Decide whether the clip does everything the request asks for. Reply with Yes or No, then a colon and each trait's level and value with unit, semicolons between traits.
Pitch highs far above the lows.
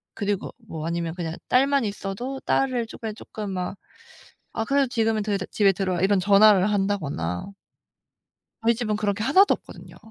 No: average, 3.2 semitones